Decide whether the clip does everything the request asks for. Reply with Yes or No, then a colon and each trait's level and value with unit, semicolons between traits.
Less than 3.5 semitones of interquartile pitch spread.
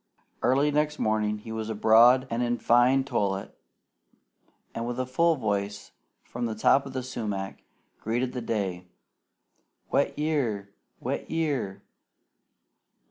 No: average, 3.8 semitones